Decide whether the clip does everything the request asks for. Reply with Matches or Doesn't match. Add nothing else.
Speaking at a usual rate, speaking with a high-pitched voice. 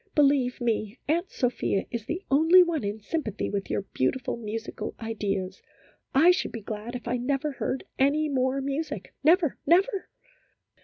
Matches